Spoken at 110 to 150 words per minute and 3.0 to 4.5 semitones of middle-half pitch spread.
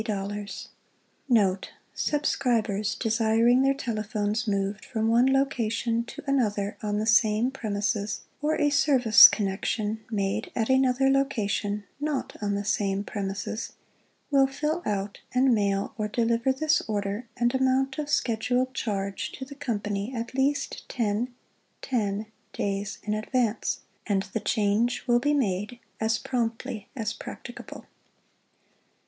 Yes: slow, 135 wpm; average, 4.0 semitones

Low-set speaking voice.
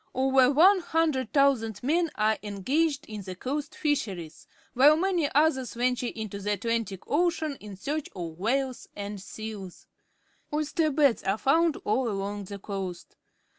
No: very high, 250 Hz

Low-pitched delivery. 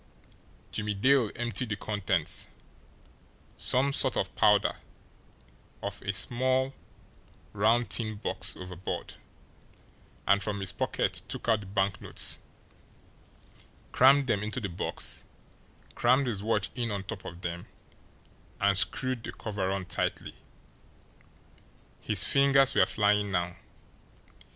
Yes: low, 105 Hz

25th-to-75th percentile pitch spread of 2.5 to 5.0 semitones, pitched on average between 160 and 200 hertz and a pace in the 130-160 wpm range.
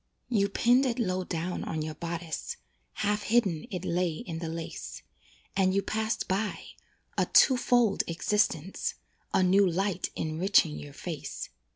Yes: average, 3.9 semitones; medium, 185 Hz; average, 150 wpm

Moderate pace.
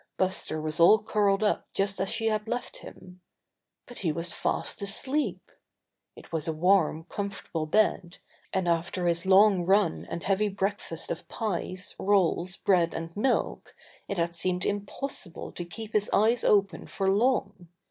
Yes: average, 160 wpm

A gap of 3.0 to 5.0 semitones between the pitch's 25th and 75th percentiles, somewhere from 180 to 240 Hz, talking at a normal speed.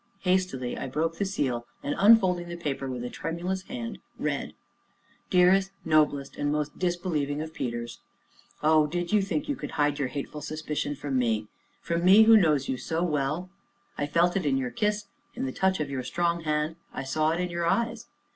No: average, 4.2 semitones; medium, 160 Hz; average, 190 wpm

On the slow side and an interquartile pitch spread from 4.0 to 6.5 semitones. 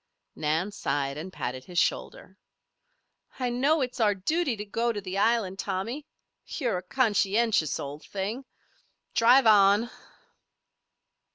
Yes: slow, 125 wpm; average, 4.6 semitones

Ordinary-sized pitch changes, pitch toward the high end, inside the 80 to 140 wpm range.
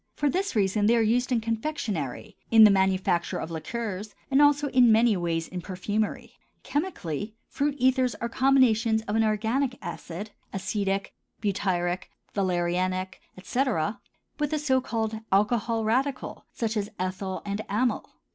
Yes: average, 4.6 semitones; high, 215 Hz; slow, 135 wpm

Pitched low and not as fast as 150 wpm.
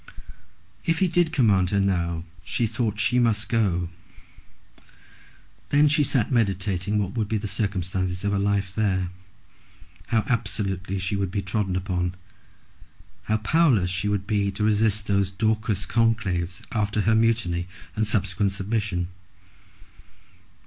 Yes: low, 100 Hz; average, 140 wpm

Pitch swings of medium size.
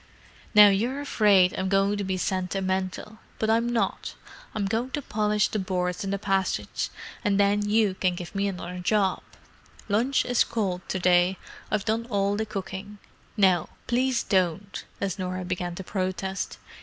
No: narrow, 2.3 semitones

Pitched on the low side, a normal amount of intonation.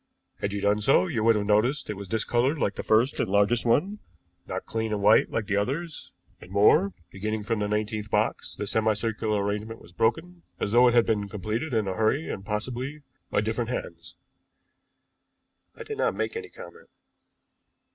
Yes: low, 110 Hz; average, 3.8 semitones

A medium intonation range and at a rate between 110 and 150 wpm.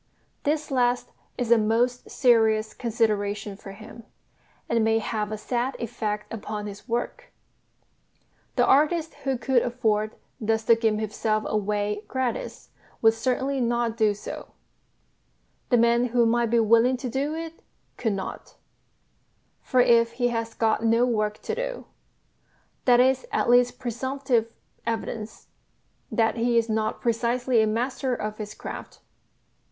No: narrow, 2.3 semitones; average, 140 wpm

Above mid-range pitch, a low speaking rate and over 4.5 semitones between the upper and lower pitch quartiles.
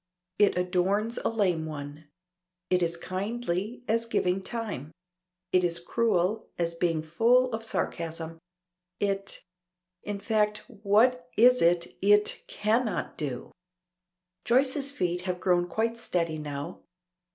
Yes: high, 195 Hz; slow, 120 wpm; average, 4.9 semitones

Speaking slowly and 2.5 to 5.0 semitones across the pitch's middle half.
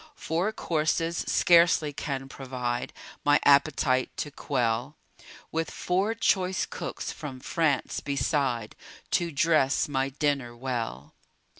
Yes: slow, 110 wpm; average, 3.9 semitones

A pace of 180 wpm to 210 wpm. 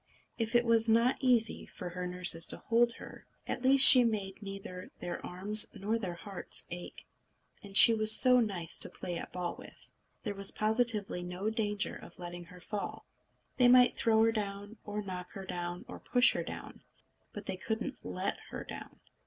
Yes: average, 185 wpm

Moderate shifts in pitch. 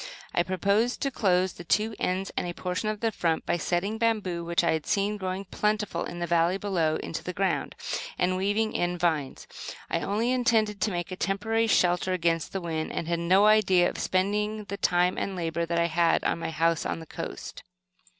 Yes: average, 3.5 semitones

